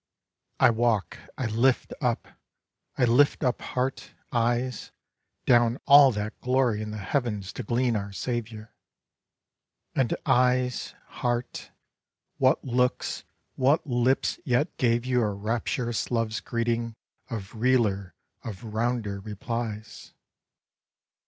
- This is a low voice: Yes, low, 120 Hz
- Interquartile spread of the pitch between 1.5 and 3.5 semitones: Yes, narrow, 2.5 semitones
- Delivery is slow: Yes, slow, 115 wpm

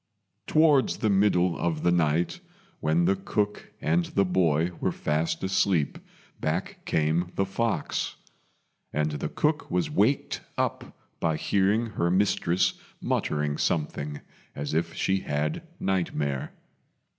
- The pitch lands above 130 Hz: No, very low, 85 Hz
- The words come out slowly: Yes, slow, 125 wpm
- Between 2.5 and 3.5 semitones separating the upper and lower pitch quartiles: No, average, 4.4 semitones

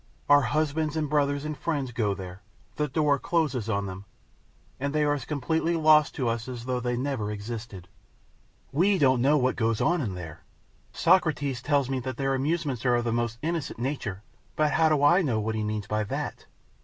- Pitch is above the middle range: No, low, 135 Hz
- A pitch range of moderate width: Yes, average, 4.8 semitones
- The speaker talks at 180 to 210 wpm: Yes, average, 200 wpm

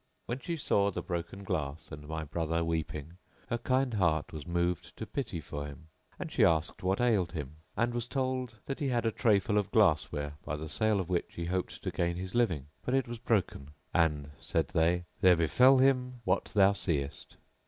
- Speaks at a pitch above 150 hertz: No, very low, 90 Hz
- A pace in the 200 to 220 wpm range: Yes, fast, 205 wpm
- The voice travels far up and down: Yes, wide, 6.6 semitones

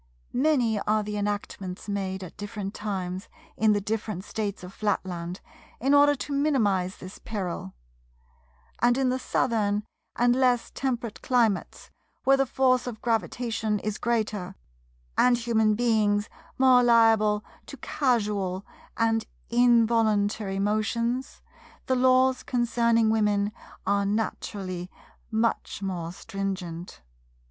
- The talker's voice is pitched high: Yes, high, 215 Hz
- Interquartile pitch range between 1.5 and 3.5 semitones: Yes, average, 3.2 semitones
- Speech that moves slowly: Yes, slow, 120 wpm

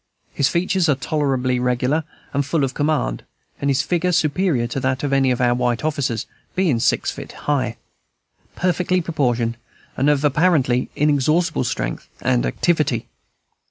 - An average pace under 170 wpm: Yes, average, 150 wpm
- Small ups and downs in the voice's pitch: No, average, 4.1 semitones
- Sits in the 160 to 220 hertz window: No, medium, 140 Hz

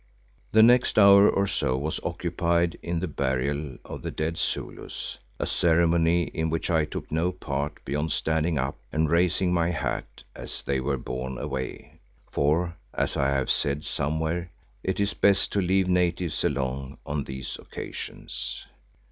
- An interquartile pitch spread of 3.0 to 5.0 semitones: Yes, average, 3.8 semitones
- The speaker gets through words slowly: No, average, 155 wpm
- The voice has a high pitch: No, very low, 80 Hz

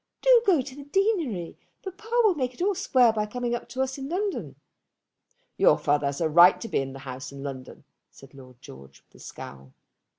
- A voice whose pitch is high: Yes, high, 230 Hz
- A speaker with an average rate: No, fast, 210 wpm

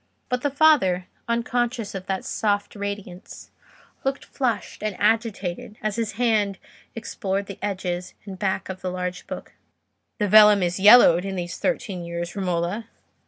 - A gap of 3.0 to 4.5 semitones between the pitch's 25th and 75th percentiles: Yes, average, 3.6 semitones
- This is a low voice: No, high, 200 Hz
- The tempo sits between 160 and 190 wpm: No, average, 150 wpm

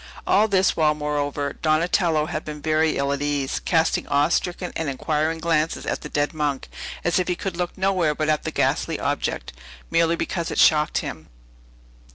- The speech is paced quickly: No, average, 185 wpm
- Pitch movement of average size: No, narrow, 2.3 semitones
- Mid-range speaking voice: Yes, medium, 155 Hz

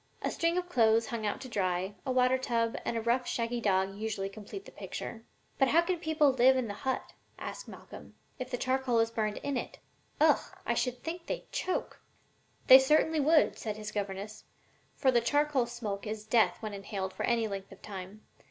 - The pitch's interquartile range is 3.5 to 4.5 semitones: Yes, average, 3.9 semitones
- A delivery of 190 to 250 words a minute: Yes, average, 200 wpm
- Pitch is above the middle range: Yes, high, 235 Hz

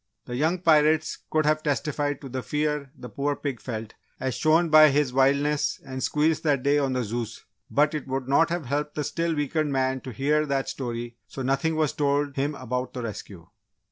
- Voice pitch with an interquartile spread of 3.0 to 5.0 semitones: No, narrow, 2.6 semitones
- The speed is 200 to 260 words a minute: Yes, fast, 205 wpm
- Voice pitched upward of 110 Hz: Yes, medium, 140 Hz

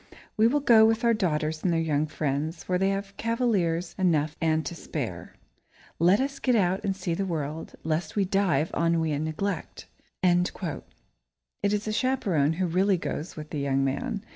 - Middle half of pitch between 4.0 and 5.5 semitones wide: Yes, average, 4.4 semitones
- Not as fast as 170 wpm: No, average, 185 wpm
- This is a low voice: No, medium, 175 Hz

